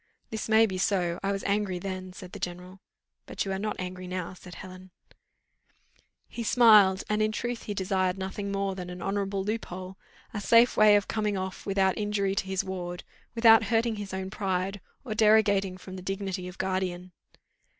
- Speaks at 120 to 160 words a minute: No, average, 185 wpm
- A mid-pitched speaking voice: No, high, 195 Hz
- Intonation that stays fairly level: Yes, narrow, 2.1 semitones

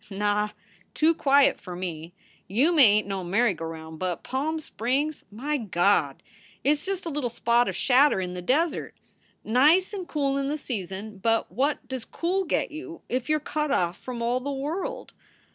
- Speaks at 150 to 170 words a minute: No, average, 190 wpm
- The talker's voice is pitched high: Yes, very high, 255 Hz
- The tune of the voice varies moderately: No, wide, 7.1 semitones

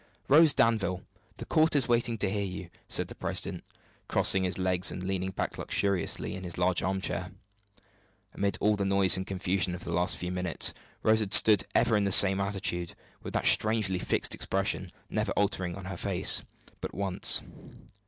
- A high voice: No, very low, 95 Hz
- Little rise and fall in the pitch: Yes, narrow, 2.0 semitones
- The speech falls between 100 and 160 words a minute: No, average, 180 wpm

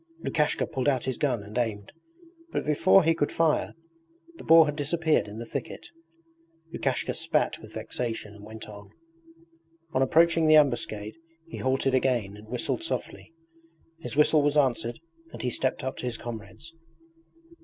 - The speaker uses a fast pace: No, average, 160 wpm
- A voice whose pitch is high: No, low, 130 Hz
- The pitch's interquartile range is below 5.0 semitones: No, average, 5.3 semitones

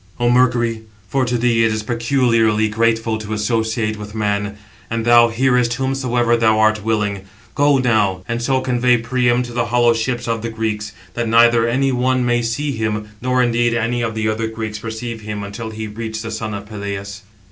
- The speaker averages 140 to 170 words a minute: No, average, 190 wpm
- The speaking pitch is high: No, low, 115 Hz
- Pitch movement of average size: No, narrow, 1.9 semitones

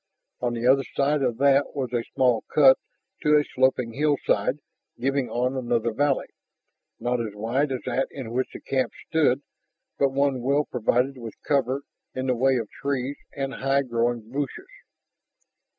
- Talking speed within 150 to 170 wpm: Yes, average, 165 wpm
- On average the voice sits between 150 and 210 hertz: No, low, 130 Hz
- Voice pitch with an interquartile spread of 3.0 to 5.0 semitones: No, narrow, 2.4 semitones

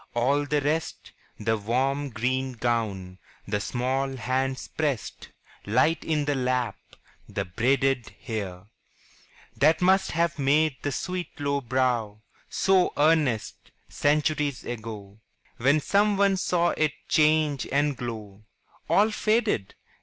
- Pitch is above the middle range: No, low, 135 Hz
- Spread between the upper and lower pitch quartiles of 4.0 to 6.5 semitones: Yes, average, 4.8 semitones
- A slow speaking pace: Yes, slow, 120 wpm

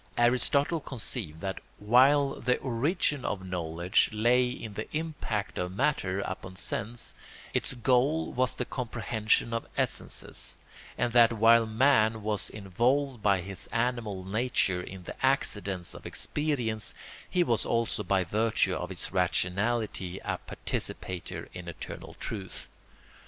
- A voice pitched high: No, low, 115 Hz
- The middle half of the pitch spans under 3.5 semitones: No, average, 4.6 semitones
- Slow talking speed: Yes, slow, 130 wpm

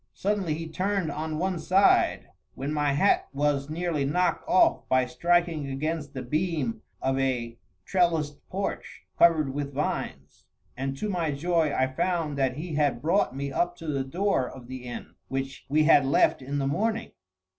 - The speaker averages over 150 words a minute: Yes, average, 170 wpm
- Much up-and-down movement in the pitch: No, average, 4.3 semitones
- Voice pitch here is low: No, medium, 150 Hz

